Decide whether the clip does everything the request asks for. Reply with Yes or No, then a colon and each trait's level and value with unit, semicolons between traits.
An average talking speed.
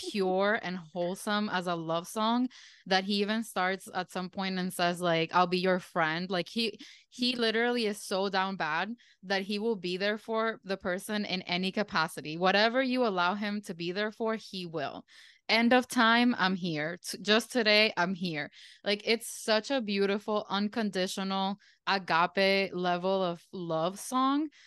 Yes: average, 175 wpm